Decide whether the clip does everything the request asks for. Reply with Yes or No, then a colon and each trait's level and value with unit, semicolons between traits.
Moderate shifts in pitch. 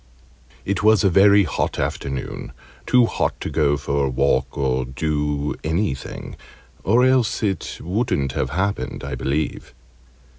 No: wide, 6.8 semitones